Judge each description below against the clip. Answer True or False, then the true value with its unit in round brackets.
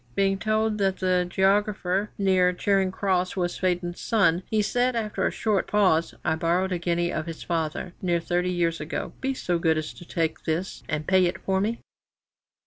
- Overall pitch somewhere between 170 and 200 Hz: True (185 Hz)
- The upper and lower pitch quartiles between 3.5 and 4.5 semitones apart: False (2.5 semitones)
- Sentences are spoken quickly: False (190 wpm)